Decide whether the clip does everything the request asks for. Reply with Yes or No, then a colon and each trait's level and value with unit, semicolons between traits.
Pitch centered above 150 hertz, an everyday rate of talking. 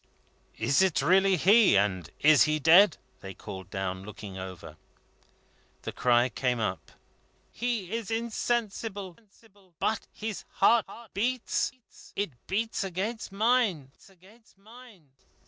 No: high, 190 Hz; slow, 110 wpm